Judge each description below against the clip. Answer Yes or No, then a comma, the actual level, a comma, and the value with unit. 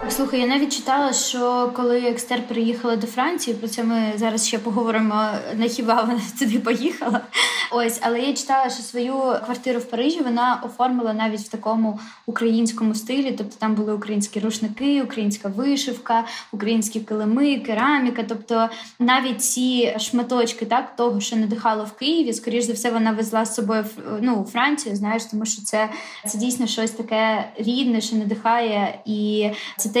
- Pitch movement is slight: Yes, narrow, 2.0 semitones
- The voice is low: No, high, 230 Hz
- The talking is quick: Yes, fast, 160 wpm